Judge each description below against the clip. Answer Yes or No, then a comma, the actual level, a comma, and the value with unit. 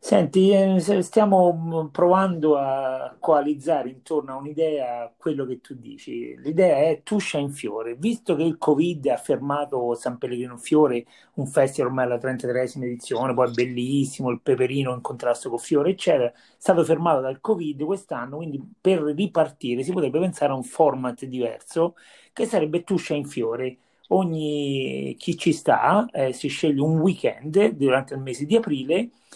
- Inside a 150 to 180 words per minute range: Yes, average, 155 wpm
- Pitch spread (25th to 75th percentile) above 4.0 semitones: Yes, average, 5.2 semitones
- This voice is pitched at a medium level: Yes, medium, 150 Hz